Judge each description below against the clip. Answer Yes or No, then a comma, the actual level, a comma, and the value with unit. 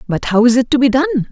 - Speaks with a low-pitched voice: No, very high, 255 Hz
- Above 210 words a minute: Yes, fast, 320 wpm